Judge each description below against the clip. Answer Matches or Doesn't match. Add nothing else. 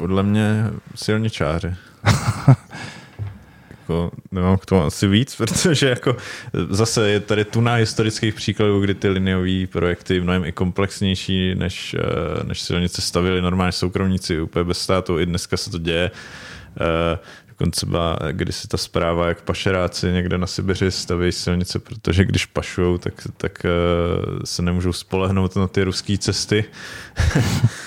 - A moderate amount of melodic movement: Matches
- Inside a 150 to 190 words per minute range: Doesn't match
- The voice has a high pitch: Doesn't match